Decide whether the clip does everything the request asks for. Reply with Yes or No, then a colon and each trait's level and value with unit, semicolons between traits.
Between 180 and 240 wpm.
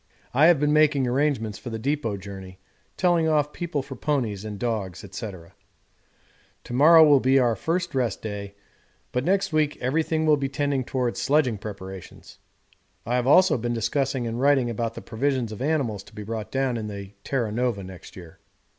Yes: average, 185 wpm